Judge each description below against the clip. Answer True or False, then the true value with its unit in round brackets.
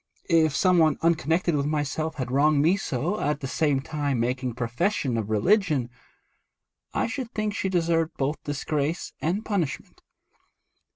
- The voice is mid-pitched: True (155 Hz)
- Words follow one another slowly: False (150 wpm)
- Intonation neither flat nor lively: True (4.1 semitones)